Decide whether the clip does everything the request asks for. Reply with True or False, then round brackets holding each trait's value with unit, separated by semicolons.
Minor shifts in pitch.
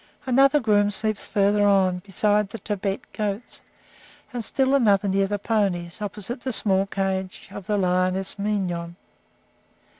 True (2.1 semitones)